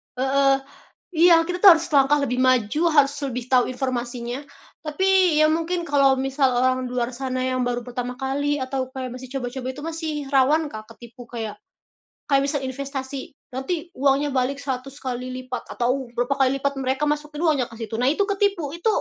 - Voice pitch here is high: Yes, very high, 270 Hz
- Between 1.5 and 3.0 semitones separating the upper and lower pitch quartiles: Yes, average, 2.7 semitones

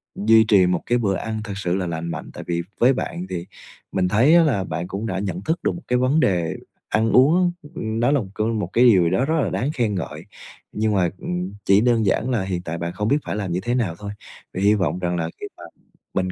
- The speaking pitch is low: Yes, low, 100 Hz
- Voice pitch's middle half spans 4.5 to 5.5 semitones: Yes, average, 4.9 semitones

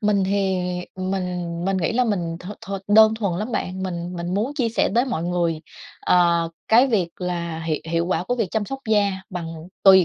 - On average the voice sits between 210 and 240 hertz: No, high, 190 Hz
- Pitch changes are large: No, average, 3.5 semitones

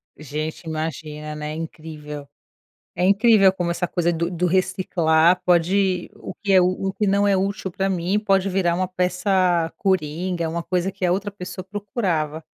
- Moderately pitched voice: Yes, medium, 180 Hz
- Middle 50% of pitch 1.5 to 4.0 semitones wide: Yes, average, 3.0 semitones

